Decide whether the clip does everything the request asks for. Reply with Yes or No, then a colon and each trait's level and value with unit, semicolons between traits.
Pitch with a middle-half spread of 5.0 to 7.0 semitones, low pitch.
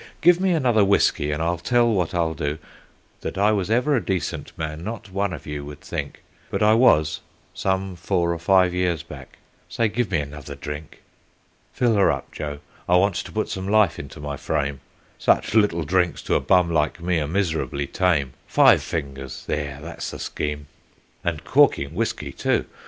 Yes: average, 5.3 semitones; very low, 85 Hz